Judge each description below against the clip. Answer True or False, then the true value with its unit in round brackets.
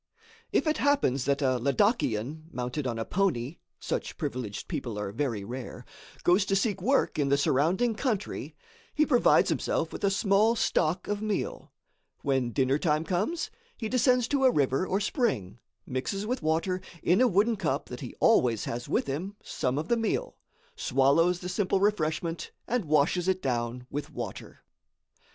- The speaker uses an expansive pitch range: True (7.8 semitones)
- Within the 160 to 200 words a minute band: True (170 wpm)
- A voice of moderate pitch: True (165 Hz)